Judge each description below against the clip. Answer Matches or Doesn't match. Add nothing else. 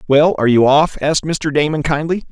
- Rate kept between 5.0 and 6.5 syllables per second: Matches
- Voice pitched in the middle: Matches